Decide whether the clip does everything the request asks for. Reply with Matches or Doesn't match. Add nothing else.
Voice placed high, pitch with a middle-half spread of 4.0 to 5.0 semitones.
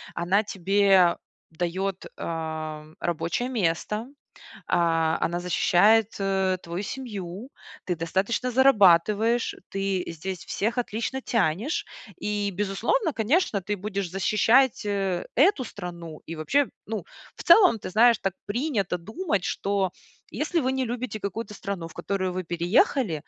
Matches